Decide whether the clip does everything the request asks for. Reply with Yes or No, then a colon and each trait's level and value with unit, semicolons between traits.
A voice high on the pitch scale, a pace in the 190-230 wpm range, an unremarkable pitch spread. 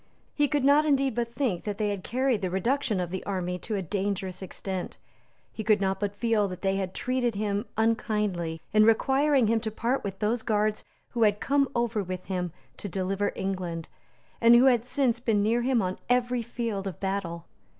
Yes: high, 210 Hz; average, 200 wpm; average, 3.8 semitones